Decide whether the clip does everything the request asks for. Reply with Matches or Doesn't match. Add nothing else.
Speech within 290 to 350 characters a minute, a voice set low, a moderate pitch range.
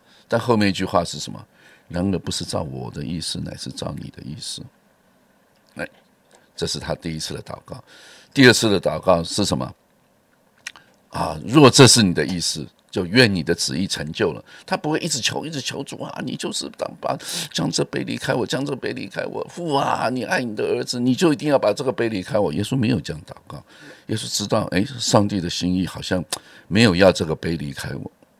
Doesn't match